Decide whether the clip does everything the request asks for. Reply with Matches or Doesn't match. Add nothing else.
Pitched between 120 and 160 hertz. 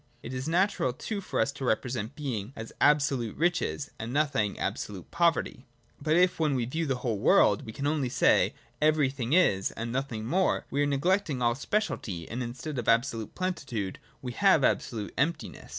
Matches